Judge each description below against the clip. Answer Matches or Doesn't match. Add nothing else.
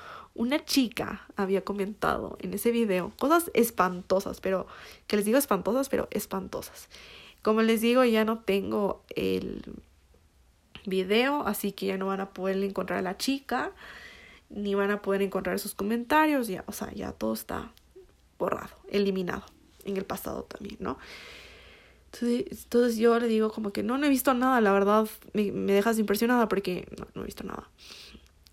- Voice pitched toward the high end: Matches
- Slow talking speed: Doesn't match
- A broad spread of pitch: Doesn't match